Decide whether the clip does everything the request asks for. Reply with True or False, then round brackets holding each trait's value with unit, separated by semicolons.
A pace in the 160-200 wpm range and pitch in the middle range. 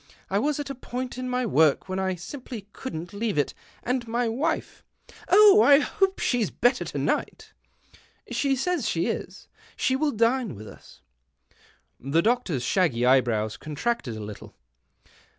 False (170 wpm; 230 Hz)